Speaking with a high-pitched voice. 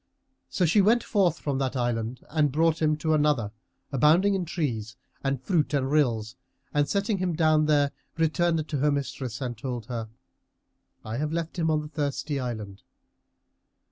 No: medium, 150 Hz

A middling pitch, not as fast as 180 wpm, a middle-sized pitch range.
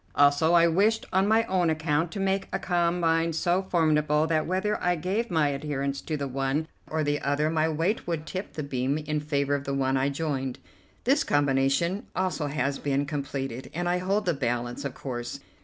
No: medium, 155 Hz; average, 195 wpm; average, 3.9 semitones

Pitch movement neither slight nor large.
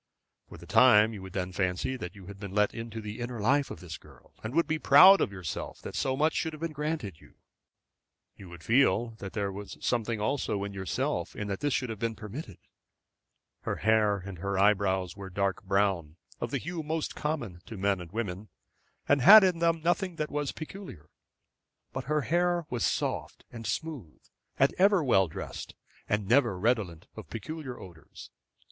No: wide, 7.0 semitones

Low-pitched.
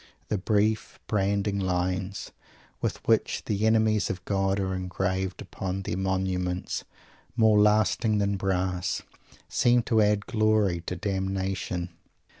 Yes: very low, 95 Hz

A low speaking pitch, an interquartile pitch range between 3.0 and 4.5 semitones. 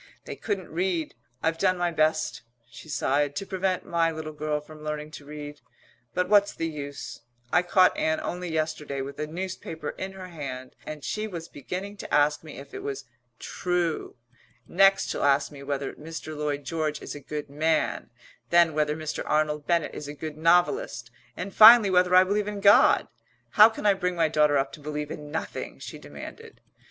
No: medium, 160 Hz; average, 3.4 semitones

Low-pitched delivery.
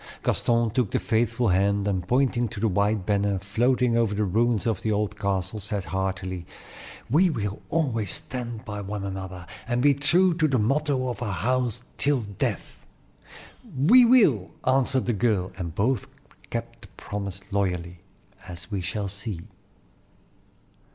Yes: low, 110 Hz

